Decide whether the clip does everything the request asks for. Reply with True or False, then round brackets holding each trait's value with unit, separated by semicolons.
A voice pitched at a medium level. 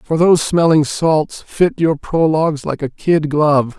True (155 Hz)